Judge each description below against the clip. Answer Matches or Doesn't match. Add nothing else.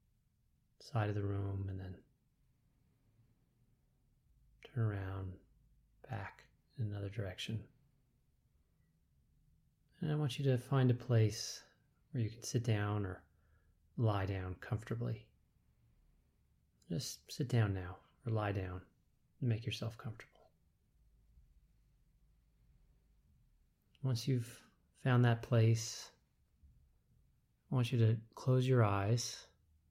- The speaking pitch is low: Matches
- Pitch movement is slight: Doesn't match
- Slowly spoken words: Matches